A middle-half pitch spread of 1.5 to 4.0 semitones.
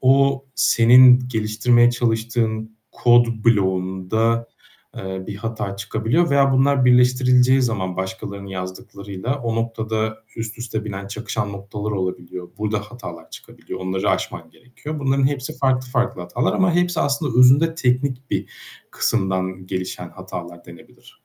No: average, 4.4 semitones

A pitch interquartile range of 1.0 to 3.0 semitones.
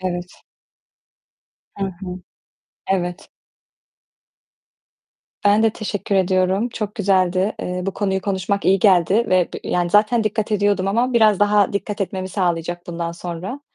Yes: narrow, 2.4 semitones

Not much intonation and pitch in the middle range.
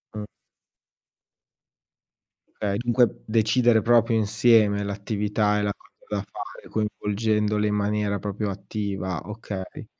No: narrow, 1.4 semitones; low, 105 Hz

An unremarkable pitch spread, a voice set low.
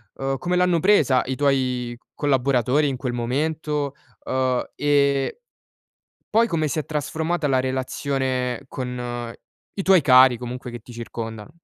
Yes: average, 3.0 semitones; low, 130 Hz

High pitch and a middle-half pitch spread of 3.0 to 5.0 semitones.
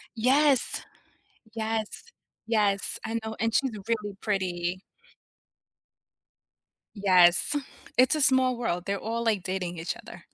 Yes: high, 220 Hz; average, 3.9 semitones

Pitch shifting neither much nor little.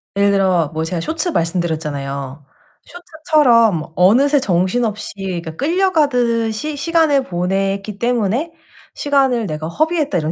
No: wide, 8.7 semitones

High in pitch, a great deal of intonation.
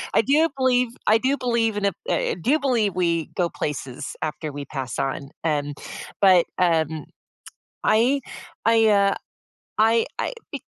Yes: high, 200 Hz; wide, 7.2 semitones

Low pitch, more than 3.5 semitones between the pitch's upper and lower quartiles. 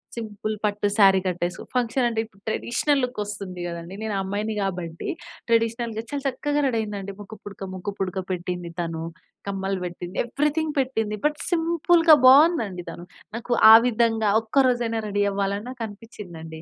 No: high, 215 Hz; average, 4.1 semitones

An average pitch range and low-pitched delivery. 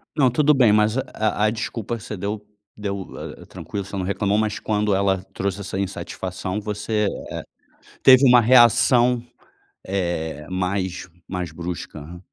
Yes: average, 3.0 semitones; low, 100 Hz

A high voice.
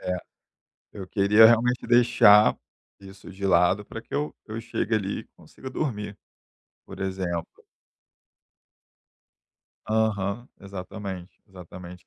No: low, 100 Hz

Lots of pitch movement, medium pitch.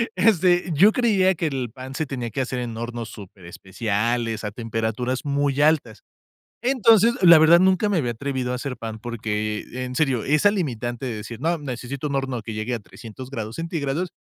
No: wide, 5.8 semitones; low, 130 Hz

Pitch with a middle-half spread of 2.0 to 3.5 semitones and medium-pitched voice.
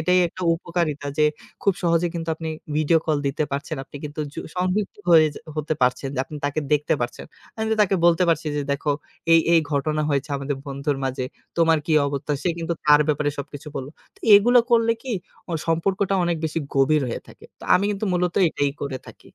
Yes: average, 3.2 semitones; medium, 155 Hz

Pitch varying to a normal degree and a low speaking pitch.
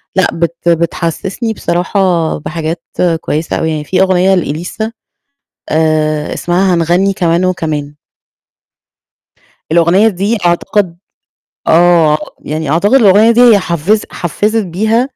No: average, 3.4 semitones; medium, 175 Hz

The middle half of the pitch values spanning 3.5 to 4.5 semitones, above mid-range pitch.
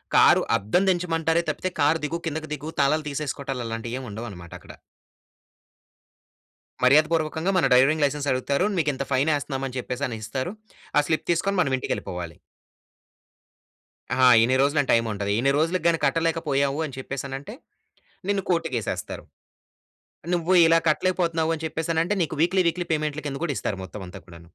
No: average, 4.0 semitones; medium, 145 Hz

